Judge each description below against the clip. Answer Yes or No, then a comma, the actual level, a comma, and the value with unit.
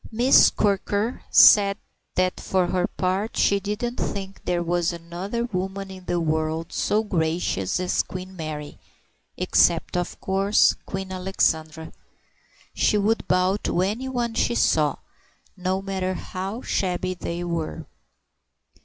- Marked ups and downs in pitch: No, narrow, 2.5 semitones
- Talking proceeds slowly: Yes, slow, 125 wpm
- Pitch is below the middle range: No, medium, 185 Hz